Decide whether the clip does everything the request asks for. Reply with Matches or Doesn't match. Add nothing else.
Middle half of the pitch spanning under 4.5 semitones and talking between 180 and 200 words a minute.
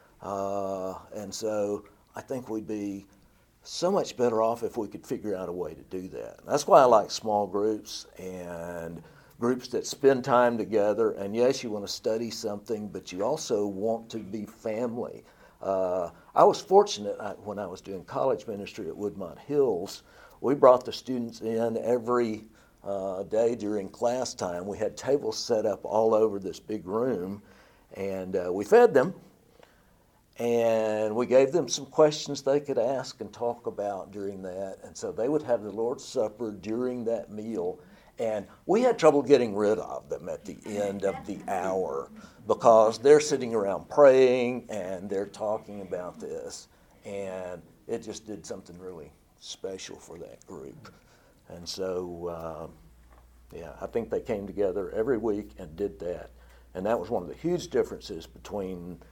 Doesn't match